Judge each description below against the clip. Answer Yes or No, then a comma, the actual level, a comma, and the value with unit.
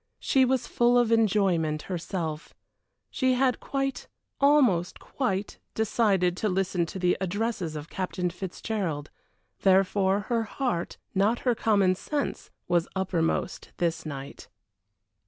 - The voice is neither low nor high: No, high, 195 Hz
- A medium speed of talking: No, slow, 120 wpm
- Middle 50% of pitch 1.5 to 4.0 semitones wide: No, average, 5.1 semitones